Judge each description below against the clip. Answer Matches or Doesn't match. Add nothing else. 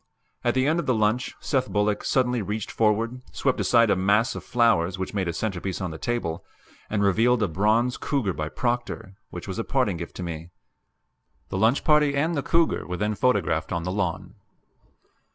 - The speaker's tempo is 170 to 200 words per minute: Matches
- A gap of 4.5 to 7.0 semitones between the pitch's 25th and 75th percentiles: Matches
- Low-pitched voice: Matches